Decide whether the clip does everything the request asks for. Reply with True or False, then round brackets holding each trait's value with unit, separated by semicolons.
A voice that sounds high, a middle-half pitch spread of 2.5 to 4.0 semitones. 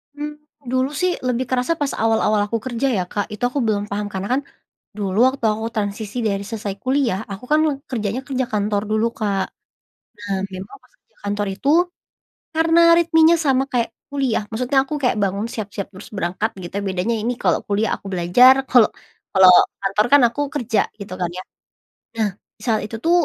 False (220 Hz; 4.5 semitones)